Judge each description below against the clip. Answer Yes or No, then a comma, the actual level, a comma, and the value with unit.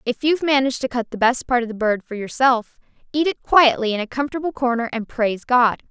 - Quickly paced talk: Yes, fast, 235 wpm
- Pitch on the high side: Yes, very high, 250 Hz